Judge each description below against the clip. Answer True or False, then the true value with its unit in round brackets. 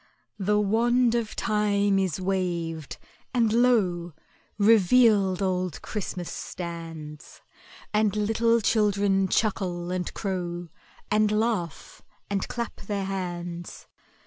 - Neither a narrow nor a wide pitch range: True (3.3 semitones)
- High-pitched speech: True (195 Hz)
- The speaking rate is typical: False (100 wpm)